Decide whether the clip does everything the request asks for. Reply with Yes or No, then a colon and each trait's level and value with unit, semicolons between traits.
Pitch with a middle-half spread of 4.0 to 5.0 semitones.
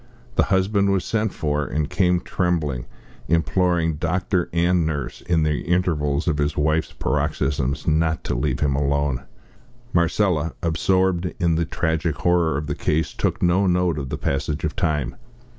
No: average, 3.2 semitones